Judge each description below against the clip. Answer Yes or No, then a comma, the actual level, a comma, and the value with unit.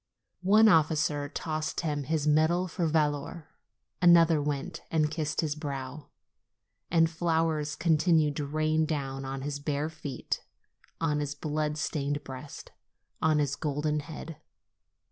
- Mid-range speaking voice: Yes, medium, 150 Hz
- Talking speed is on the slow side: Yes, slow, 130 wpm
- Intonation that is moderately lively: No, narrow, 1.7 semitones